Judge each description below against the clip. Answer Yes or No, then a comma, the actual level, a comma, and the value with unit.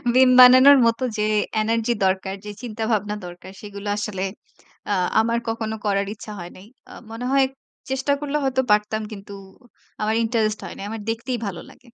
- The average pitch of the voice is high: Yes, high, 220 Hz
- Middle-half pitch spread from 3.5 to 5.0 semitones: No, average, 2.9 semitones